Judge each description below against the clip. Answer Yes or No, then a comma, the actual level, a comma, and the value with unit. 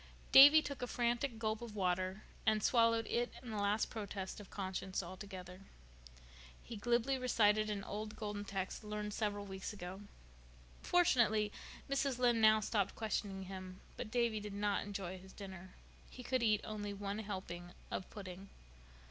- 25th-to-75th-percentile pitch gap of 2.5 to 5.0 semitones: Yes, average, 3.0 semitones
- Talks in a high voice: Yes, high, 210 Hz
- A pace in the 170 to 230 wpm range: No, average, 155 wpm